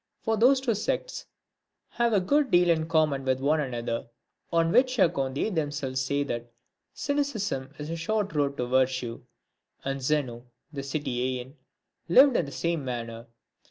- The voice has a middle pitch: Yes, medium, 145 Hz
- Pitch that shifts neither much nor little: No, wide, 6.7 semitones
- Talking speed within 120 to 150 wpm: No, average, 160 wpm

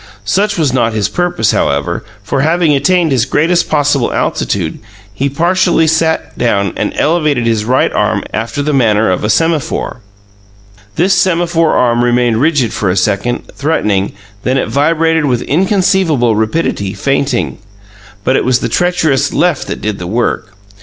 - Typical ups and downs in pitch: No, wide, 6.4 semitones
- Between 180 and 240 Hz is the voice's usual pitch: No, low, 135 Hz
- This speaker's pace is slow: No, average, 155 wpm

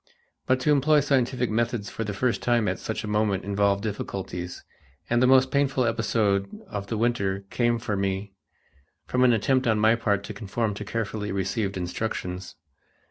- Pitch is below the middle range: Yes, low, 110 Hz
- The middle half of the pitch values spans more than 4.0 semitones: No, average, 3.3 semitones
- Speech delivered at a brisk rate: No, average, 175 wpm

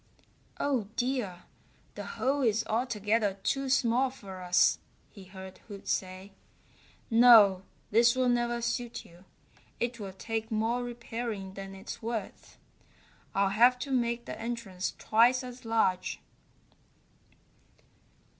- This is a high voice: Yes, high, 230 Hz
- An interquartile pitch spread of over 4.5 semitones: No, average, 3.7 semitones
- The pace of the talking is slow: Yes, slow, 120 wpm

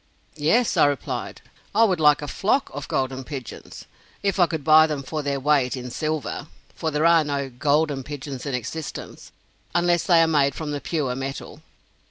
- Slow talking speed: No, average, 185 wpm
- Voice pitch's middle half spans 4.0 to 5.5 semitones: No, average, 2.8 semitones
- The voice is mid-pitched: Yes, medium, 150 Hz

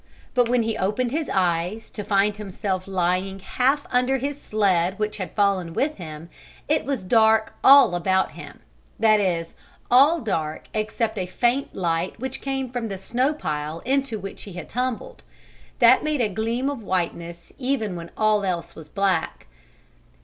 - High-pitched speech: Yes, high, 210 Hz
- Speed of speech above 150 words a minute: Yes, average, 165 wpm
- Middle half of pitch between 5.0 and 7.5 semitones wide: Yes, wide, 5.4 semitones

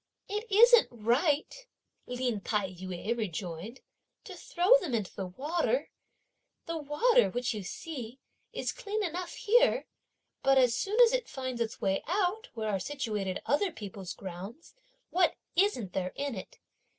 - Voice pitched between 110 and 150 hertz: No, very high, 260 Hz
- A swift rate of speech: No, average, 150 wpm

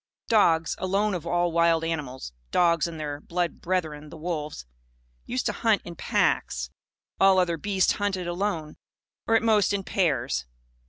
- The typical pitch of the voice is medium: Yes, medium, 170 Hz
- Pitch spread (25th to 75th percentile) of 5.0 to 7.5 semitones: No, average, 3.6 semitones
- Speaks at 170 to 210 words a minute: No, average, 155 wpm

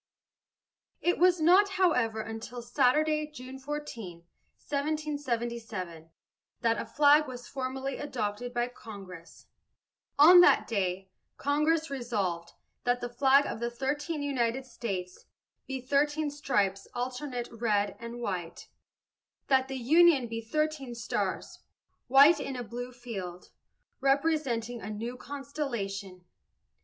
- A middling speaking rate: No, slow, 115 wpm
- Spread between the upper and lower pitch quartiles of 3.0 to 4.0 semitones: No, average, 4.4 semitones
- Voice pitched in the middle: No, very high, 250 Hz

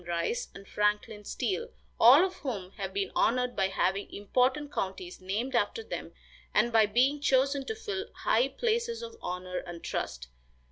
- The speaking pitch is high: Yes, high, 235 Hz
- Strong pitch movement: Yes, wide, 7.1 semitones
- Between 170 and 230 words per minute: No, average, 160 wpm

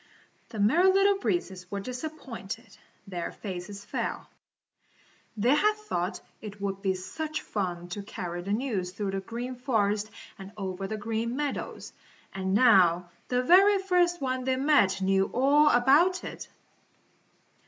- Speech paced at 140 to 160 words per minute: Yes, average, 145 wpm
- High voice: Yes, high, 220 Hz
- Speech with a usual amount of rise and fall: No, wide, 6.6 semitones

